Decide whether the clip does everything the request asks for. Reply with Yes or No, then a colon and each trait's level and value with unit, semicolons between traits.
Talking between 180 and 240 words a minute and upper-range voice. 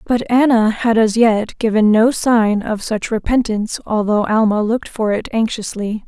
No: average, 170 wpm; high, 220 Hz